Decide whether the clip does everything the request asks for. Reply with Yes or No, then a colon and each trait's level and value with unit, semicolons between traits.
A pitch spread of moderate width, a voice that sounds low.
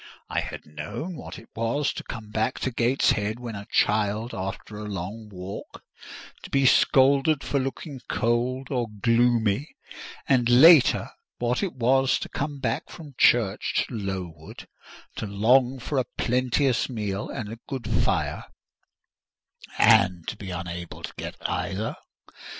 Yes: average, 4.3 semitones; low, 115 Hz